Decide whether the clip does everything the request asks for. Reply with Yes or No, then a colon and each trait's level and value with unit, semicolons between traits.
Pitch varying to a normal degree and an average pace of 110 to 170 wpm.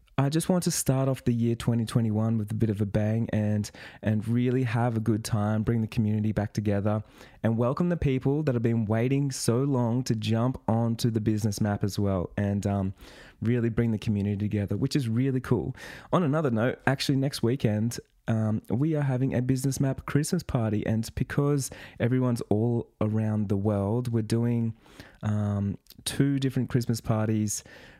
No: average, 3.4 semitones; average, 180 wpm